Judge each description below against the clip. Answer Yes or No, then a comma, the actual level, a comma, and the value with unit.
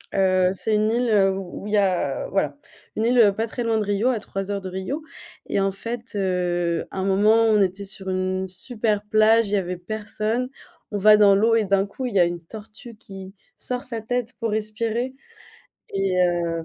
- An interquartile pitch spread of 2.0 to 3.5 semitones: Yes, average, 2.9 semitones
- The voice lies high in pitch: Yes, high, 205 Hz